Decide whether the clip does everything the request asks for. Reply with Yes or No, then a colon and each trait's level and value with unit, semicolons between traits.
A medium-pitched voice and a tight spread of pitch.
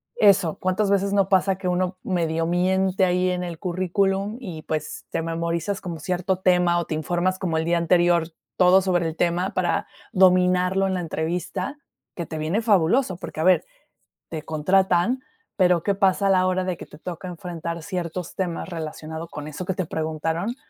Yes: medium, 180 Hz; narrow, 2.1 semitones